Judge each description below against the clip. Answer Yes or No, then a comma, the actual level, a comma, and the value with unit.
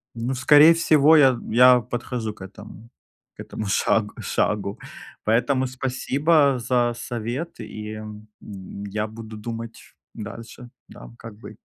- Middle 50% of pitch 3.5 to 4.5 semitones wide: No, average, 3.1 semitones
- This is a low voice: Yes, low, 115 Hz